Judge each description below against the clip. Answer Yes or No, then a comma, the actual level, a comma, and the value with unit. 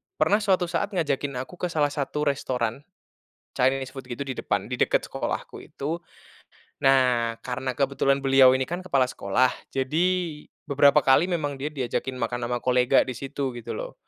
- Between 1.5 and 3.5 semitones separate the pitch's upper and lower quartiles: Yes, average, 2.8 semitones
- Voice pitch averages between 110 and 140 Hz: Yes, low, 135 Hz